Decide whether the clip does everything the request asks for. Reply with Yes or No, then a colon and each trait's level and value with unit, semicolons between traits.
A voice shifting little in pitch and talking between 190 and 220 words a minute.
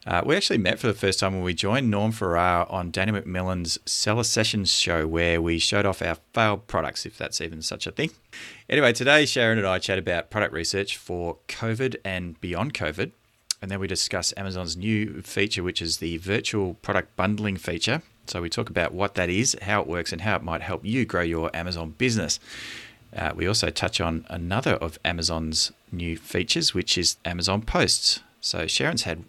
No: average, 4.0 semitones; average, 200 wpm